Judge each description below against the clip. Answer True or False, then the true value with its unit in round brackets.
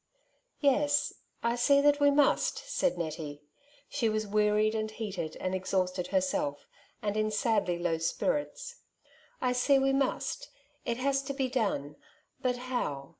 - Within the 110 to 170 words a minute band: True (160 wpm)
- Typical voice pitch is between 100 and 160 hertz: False (225 Hz)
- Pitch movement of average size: False (6.7 semitones)